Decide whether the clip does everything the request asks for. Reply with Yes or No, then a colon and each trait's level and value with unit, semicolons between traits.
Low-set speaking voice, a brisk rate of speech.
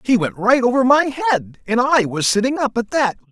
No: high, 235 Hz; fast, 235 wpm